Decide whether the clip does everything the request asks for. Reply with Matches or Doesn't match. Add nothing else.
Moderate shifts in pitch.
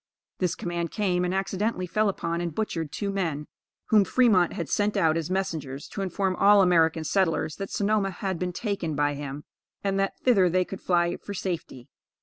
Matches